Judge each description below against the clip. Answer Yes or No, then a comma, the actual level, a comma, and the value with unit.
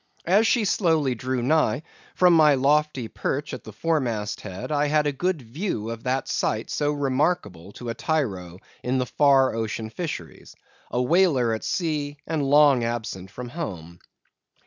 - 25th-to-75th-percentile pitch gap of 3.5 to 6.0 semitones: Yes, average, 5.0 semitones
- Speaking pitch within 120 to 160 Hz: Yes, low, 135 Hz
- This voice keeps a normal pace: Yes, average, 165 wpm